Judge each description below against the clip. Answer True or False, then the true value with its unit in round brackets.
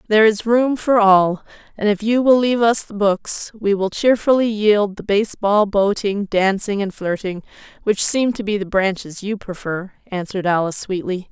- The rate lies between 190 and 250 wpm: False (180 wpm)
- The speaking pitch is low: False (205 Hz)